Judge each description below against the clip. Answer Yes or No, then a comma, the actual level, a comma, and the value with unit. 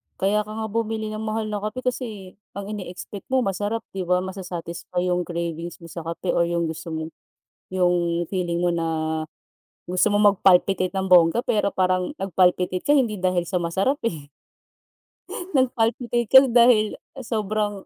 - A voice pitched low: No, high, 190 Hz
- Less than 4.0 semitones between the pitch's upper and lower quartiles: Yes, average, 3.4 semitones